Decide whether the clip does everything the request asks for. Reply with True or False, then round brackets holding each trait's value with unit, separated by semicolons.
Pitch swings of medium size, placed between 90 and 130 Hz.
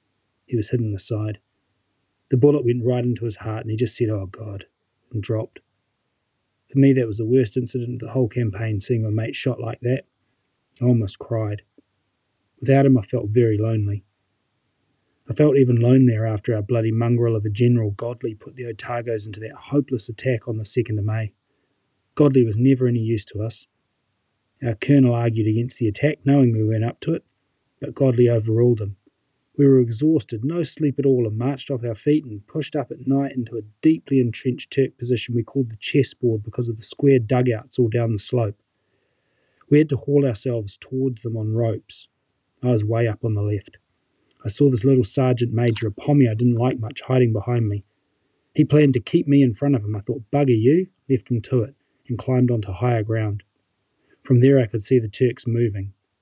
True (3.0 semitones; 120 Hz)